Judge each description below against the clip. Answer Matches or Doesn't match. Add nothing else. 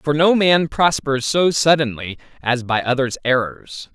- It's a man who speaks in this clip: Matches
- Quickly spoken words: Doesn't match